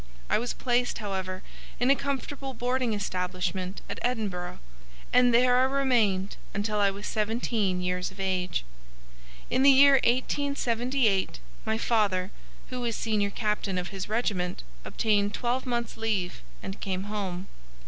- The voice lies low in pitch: No, high, 215 Hz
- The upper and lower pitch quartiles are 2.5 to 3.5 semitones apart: No, average, 4.5 semitones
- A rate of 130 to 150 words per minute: Yes, average, 140 wpm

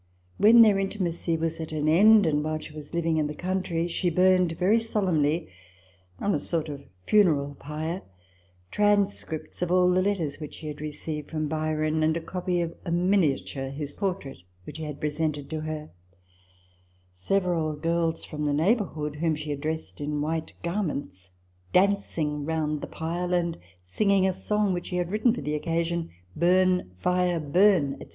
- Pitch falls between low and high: Yes, medium, 165 Hz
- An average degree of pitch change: Yes, average, 3.3 semitones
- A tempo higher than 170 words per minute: Yes, average, 180 wpm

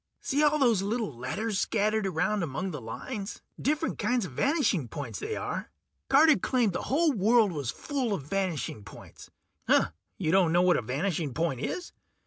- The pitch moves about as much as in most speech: No, wide, 7.8 semitones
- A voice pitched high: Yes, high, 195 Hz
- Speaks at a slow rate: No, average, 170 wpm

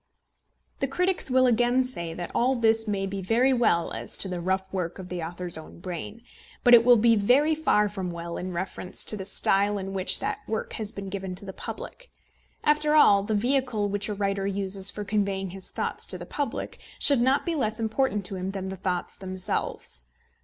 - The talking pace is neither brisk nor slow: No, fast, 210 wpm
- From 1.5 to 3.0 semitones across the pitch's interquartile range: No, average, 4.2 semitones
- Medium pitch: No, high, 200 Hz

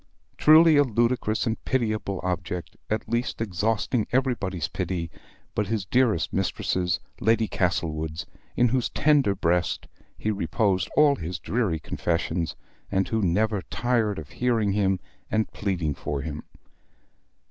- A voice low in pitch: Yes, low, 105 Hz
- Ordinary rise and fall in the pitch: Yes, average, 4.7 semitones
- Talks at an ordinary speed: No, slow, 130 wpm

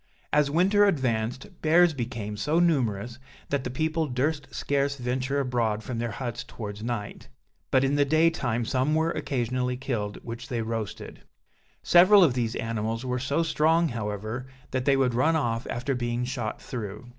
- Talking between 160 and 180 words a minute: Yes, average, 170 wpm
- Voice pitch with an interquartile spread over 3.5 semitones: Yes, average, 3.9 semitones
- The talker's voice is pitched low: Yes, low, 125 Hz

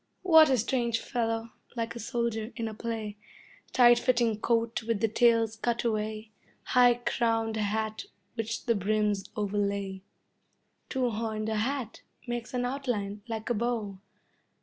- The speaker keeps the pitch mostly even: Yes, narrow, 2.0 semitones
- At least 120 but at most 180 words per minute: Yes, average, 140 wpm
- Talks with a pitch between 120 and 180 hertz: No, high, 225 Hz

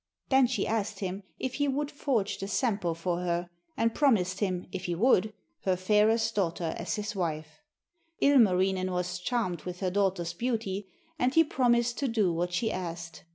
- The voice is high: Yes, high, 195 Hz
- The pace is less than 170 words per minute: No, average, 175 wpm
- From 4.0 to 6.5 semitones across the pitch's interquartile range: Yes, average, 4.7 semitones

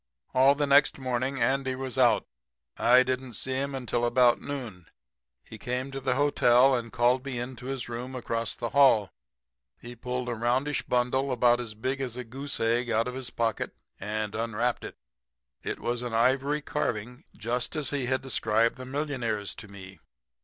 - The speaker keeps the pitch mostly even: Yes, narrow, 2.2 semitones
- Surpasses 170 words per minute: Yes, average, 180 wpm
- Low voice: Yes, low, 125 Hz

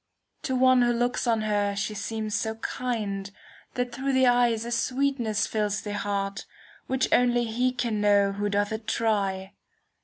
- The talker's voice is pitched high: Yes, high, 220 Hz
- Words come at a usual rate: Yes, average, 175 wpm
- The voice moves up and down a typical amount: Yes, average, 3.1 semitones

